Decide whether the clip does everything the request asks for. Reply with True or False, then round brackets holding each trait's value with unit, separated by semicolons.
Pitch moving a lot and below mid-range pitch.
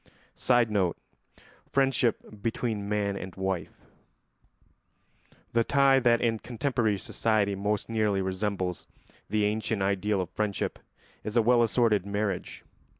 False (2.8 semitones; 105 Hz)